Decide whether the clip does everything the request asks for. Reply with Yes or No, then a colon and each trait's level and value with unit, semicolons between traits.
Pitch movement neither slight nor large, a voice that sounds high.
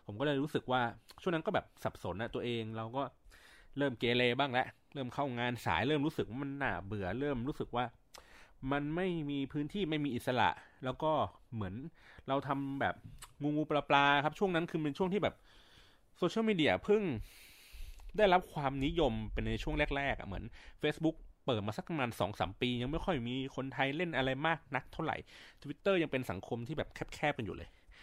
No: average, 4.2 semitones; low, 135 Hz